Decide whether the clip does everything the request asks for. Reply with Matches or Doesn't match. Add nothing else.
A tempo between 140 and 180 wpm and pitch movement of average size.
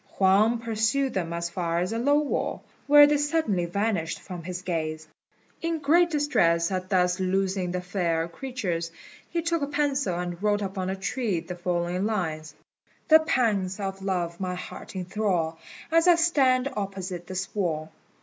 Doesn't match